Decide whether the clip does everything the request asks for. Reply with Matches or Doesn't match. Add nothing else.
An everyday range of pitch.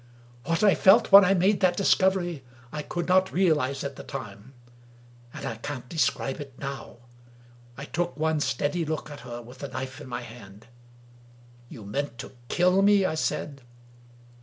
Doesn't match